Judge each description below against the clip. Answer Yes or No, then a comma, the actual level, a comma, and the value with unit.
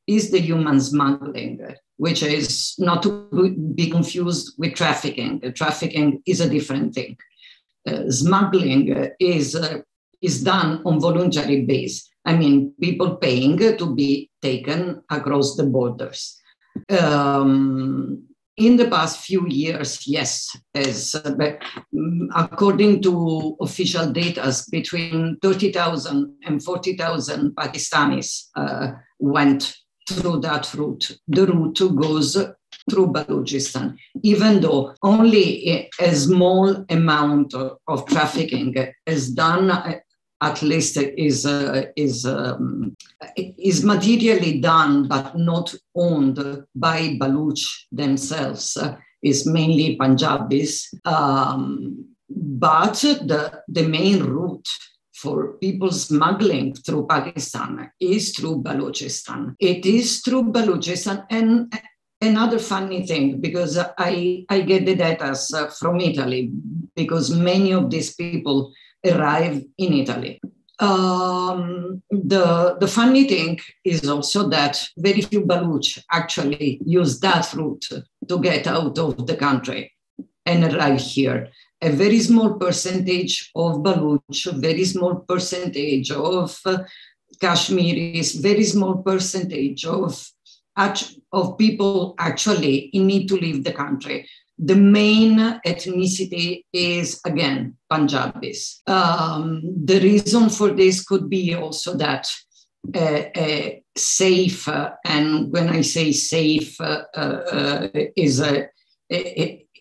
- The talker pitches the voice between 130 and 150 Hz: No, medium, 165 Hz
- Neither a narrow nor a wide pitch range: Yes, average, 4.3 semitones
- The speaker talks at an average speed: No, slow, 115 wpm